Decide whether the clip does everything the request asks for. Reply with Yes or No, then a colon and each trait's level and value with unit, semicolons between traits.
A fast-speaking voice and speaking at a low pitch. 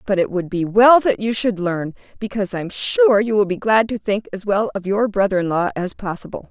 No: fast, 250 wpm; high, 200 Hz